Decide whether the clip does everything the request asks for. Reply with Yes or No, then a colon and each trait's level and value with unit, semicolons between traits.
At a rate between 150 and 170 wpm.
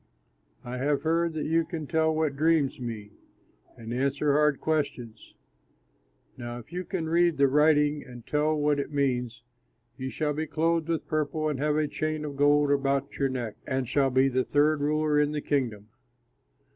No: average, 180 wpm